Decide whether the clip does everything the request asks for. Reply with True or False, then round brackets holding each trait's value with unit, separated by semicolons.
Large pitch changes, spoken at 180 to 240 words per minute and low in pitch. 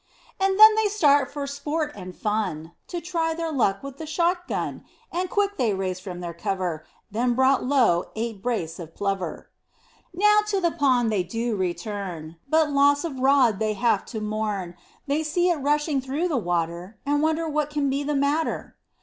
False (7.9 semitones; 185 wpm; 270 Hz)